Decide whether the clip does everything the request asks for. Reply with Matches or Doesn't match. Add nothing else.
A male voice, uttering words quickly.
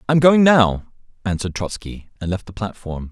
Doesn't match